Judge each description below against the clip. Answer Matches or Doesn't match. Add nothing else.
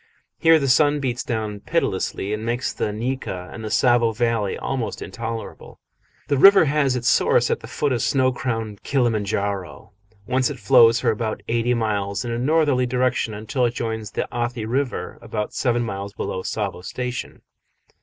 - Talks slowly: Doesn't match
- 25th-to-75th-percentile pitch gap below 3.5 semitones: Matches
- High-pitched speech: Doesn't match